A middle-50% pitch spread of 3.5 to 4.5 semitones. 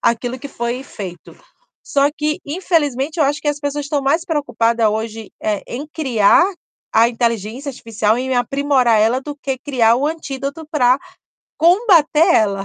Yes: average, 4.2 semitones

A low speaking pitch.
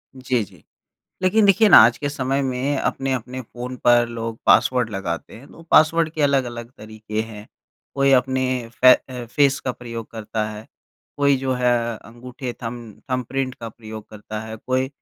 Yes: low, 125 Hz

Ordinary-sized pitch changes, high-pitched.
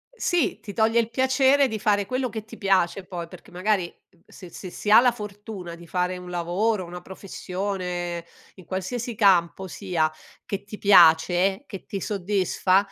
Yes: average, 3.5 semitones; high, 195 Hz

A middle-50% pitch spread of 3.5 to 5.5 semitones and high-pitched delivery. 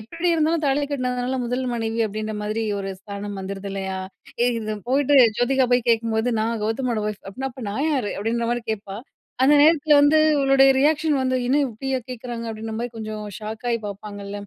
Yes: average, 3.9 semitones; high, 235 Hz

